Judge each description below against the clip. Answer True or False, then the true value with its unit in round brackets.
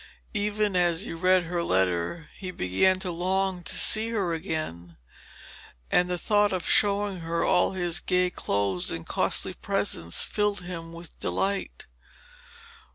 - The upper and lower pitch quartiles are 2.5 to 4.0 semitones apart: True (2.9 semitones)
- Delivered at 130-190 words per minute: True (145 wpm)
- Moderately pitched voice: True (180 Hz)